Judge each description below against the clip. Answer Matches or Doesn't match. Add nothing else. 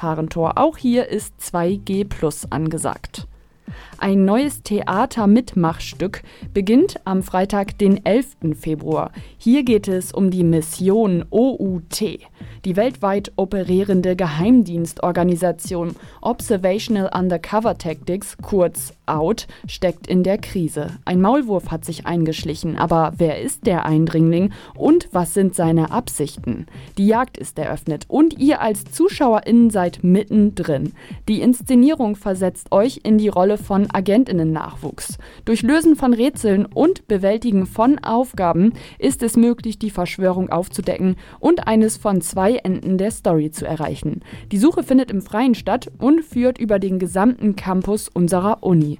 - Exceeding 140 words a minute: Doesn't match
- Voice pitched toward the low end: Doesn't match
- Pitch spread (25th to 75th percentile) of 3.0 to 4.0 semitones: Doesn't match